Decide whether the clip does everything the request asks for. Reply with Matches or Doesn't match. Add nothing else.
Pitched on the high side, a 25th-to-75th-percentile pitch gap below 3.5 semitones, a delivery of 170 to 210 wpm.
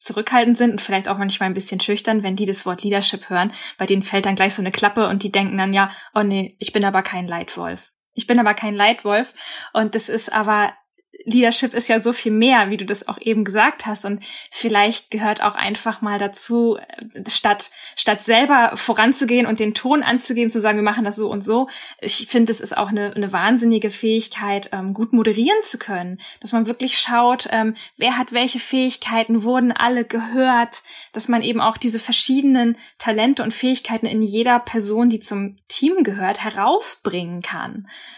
Matches